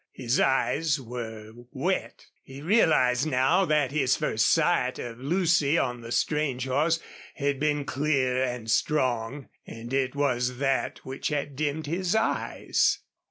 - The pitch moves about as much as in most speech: Yes, average, 3.3 semitones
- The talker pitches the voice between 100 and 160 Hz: Yes, low, 135 Hz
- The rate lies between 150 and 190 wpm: No, average, 140 wpm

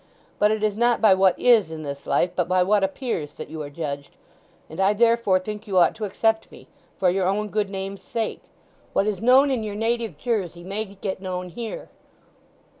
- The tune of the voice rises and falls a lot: No, average, 3.3 semitones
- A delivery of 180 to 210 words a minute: Yes, average, 200 wpm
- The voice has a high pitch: Yes, high, 200 Hz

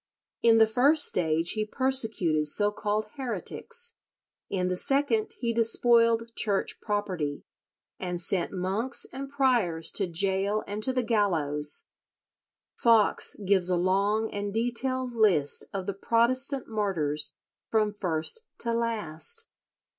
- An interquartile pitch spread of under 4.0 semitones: No, average, 4.3 semitones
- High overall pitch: Yes, high, 210 Hz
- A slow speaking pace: Yes, slow, 125 wpm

